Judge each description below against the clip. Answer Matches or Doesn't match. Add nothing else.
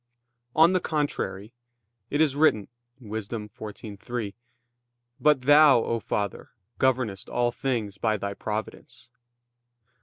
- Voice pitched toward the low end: Matches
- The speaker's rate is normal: Doesn't match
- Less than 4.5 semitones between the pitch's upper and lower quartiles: Doesn't match